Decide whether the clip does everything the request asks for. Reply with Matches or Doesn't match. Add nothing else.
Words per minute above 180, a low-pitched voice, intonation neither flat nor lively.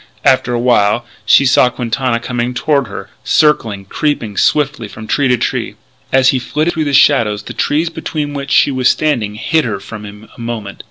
Matches